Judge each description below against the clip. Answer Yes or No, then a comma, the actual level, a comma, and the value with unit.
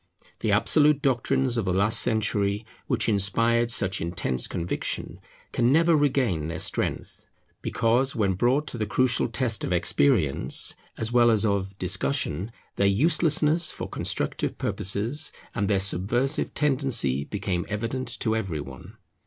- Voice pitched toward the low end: Yes, low, 110 Hz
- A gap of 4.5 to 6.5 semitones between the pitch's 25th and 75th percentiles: Yes, average, 5.2 semitones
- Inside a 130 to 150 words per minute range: Yes, average, 140 wpm